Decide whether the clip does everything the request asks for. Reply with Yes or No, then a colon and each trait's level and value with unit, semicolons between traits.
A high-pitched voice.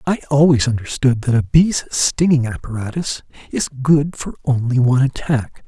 No: low, 135 Hz